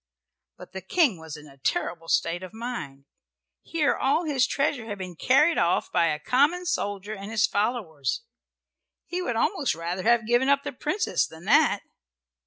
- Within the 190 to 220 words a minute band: No, average, 175 wpm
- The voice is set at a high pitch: Yes, high, 220 Hz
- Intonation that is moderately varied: No, wide, 8.2 semitones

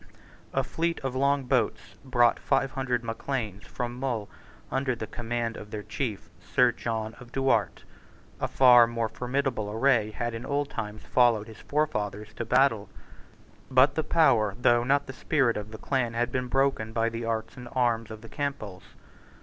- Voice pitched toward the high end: No, low, 120 Hz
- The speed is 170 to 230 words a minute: Yes, average, 175 wpm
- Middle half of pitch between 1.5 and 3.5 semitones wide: Yes, average, 3.2 semitones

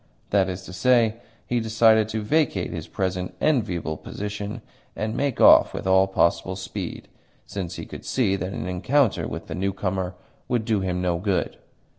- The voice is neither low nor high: No, very low, 95 Hz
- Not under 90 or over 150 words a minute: No, average, 170 wpm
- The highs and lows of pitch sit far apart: No, average, 3.3 semitones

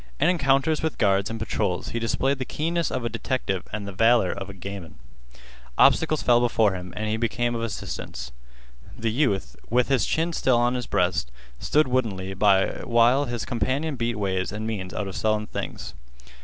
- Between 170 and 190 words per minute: Yes, average, 185 wpm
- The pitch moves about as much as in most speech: Yes, average, 4.5 semitones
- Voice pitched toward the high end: No, low, 115 Hz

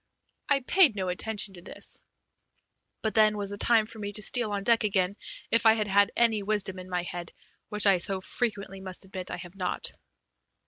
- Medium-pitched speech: No, high, 205 Hz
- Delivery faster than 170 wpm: Yes, average, 200 wpm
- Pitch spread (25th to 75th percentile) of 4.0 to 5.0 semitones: No, narrow, 2.6 semitones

